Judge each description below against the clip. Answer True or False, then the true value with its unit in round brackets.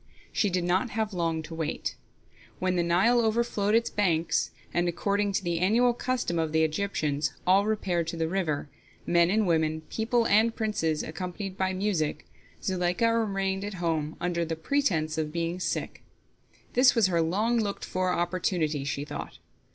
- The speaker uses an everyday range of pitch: True (4.1 semitones)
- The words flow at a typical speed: True (165 wpm)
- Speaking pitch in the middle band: True (180 Hz)